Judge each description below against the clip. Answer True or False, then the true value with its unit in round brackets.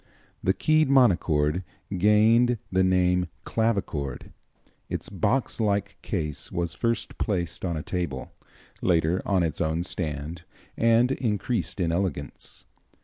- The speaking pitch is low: True (95 Hz)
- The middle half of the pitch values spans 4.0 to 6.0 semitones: True (5.0 semitones)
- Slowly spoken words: True (120 wpm)